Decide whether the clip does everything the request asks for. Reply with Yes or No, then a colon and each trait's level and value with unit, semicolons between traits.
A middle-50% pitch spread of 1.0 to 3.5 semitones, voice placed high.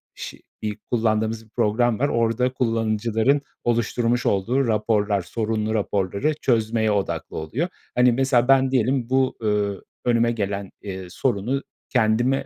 No: average, 2.8 semitones; low, 115 Hz